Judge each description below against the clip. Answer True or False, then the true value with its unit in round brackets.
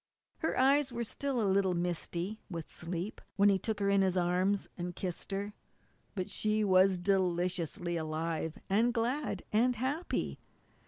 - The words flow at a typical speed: True (155 wpm)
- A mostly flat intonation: False (3.8 semitones)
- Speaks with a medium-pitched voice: False (195 Hz)